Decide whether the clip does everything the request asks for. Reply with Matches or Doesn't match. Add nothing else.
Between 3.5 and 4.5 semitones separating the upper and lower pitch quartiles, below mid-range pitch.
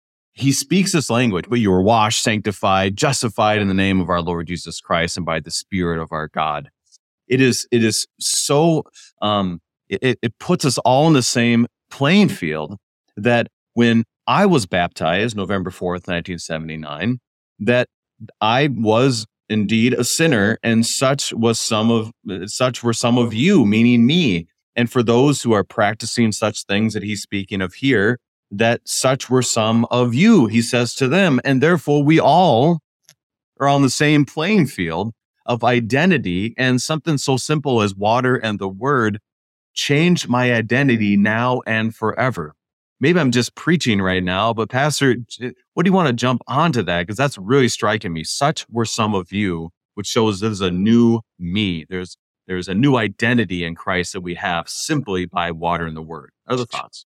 Doesn't match